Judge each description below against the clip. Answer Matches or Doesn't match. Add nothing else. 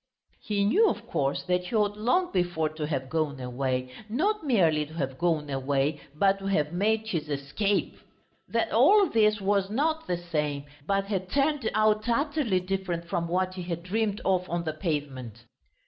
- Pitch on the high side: Doesn't match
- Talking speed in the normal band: Matches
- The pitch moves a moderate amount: Doesn't match